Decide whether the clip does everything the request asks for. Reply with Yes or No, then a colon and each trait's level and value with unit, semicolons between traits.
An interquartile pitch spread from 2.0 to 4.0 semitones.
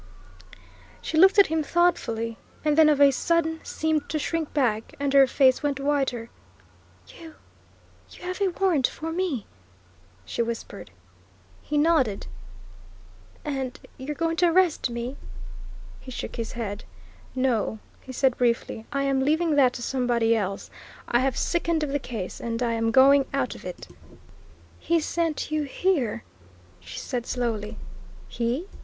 No: average, 5.0 semitones